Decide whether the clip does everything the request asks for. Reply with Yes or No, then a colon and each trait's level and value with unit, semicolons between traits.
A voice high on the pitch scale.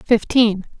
Yes: high, 220 Hz